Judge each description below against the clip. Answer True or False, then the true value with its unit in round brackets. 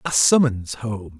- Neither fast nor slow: True (150 wpm)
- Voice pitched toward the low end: True (110 Hz)